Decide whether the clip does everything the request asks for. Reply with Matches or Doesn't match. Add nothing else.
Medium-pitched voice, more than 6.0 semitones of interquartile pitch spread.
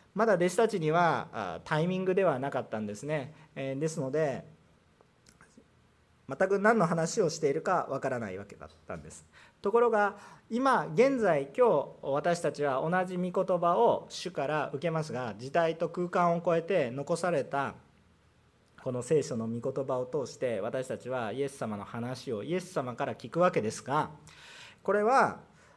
Doesn't match